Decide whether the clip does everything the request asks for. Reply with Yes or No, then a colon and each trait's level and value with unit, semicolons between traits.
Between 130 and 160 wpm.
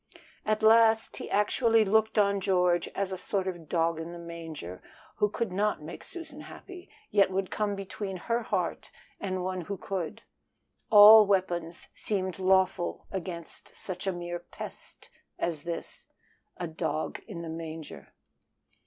Yes: average, 150 wpm